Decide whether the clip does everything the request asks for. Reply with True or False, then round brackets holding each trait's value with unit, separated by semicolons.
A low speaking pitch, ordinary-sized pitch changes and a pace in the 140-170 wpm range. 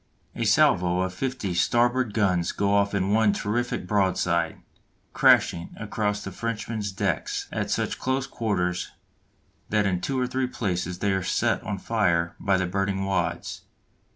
True (100 Hz; 3.4 semitones; 155 wpm)